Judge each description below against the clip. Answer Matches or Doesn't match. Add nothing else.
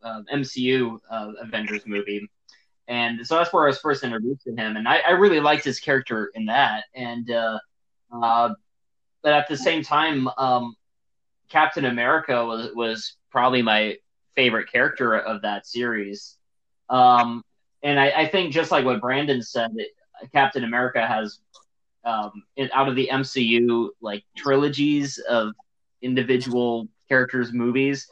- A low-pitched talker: Matches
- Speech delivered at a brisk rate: Doesn't match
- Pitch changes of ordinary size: Matches